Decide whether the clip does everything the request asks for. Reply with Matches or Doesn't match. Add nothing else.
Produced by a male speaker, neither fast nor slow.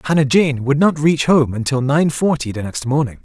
Doesn't match